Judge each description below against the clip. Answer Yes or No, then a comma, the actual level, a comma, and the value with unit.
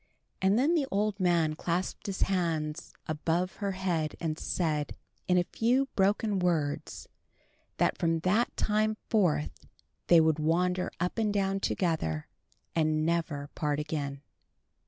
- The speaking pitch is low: No, medium, 175 Hz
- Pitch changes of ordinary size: Yes, average, 4.0 semitones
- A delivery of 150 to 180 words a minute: No, slow, 135 wpm